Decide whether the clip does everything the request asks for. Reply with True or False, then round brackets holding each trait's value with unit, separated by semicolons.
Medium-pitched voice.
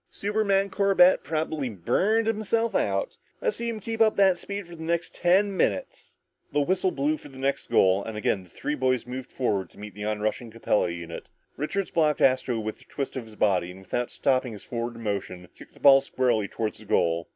False (130 Hz)